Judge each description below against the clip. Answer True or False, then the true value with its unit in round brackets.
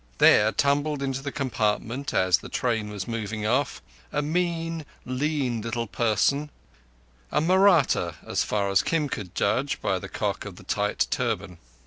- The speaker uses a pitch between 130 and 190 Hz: False (120 Hz)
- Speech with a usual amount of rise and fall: False (5.9 semitones)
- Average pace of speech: True (150 wpm)